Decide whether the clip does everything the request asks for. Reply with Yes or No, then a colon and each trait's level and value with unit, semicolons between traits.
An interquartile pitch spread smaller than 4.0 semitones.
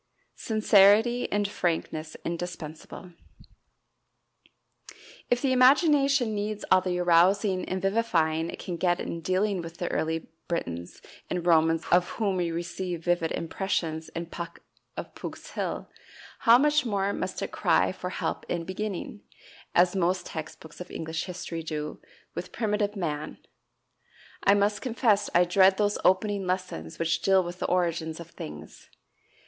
Yes: average, 3.5 semitones